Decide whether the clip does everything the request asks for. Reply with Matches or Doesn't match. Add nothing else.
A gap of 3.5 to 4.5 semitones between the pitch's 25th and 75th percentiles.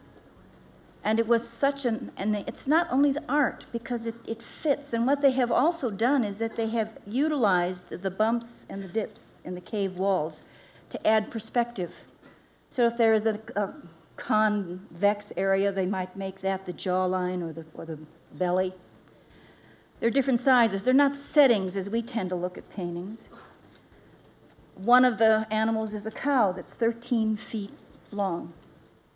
Matches